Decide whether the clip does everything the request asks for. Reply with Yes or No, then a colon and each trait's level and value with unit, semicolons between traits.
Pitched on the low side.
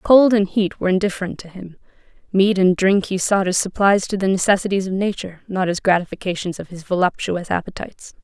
No: high, 190 Hz